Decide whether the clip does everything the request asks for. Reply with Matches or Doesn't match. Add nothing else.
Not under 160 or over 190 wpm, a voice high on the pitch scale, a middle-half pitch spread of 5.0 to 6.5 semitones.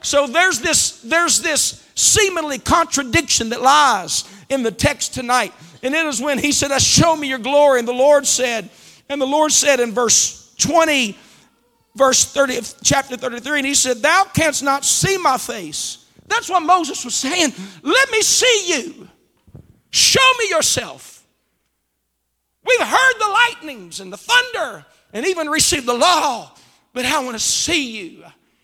Matches